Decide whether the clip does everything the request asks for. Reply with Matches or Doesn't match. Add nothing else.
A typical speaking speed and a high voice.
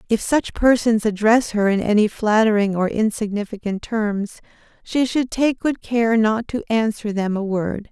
Matches